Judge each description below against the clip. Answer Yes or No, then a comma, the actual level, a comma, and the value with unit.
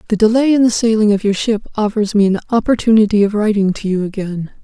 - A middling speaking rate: No, fast, 220 wpm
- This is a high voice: Yes, high, 210 Hz